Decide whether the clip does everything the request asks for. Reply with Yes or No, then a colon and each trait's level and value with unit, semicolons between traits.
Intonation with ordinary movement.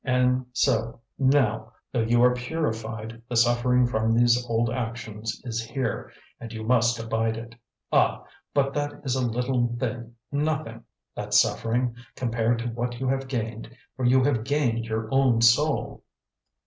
No: narrow, 2.0 semitones